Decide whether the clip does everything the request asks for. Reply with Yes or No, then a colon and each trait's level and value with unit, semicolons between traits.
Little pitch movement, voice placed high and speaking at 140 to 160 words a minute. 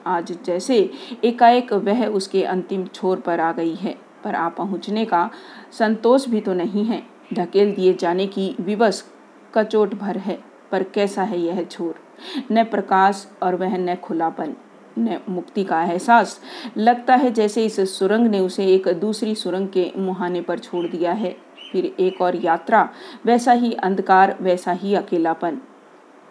No: average, 3.6 semitones; high, 195 Hz; average, 155 wpm